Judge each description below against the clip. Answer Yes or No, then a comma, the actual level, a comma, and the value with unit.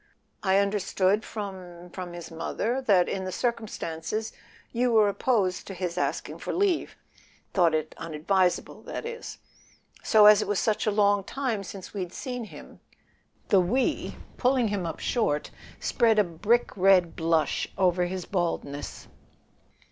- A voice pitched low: No, high, 195 Hz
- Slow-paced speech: No, average, 150 wpm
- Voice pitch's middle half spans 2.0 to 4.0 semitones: Yes, average, 3.7 semitones